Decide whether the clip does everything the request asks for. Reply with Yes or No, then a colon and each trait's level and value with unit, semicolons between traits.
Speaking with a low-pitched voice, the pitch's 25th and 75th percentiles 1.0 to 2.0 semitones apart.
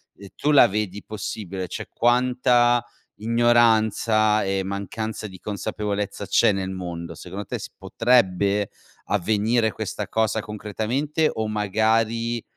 No: low, 110 Hz; narrow, 2.6 semitones